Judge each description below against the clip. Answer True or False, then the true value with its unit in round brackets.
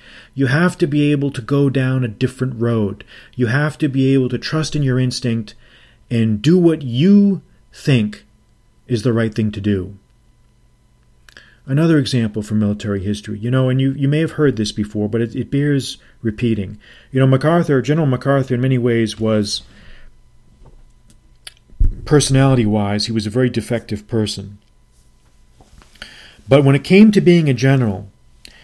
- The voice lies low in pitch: True (125 Hz)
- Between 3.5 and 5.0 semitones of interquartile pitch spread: True (4.1 semitones)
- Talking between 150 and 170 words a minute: True (160 wpm)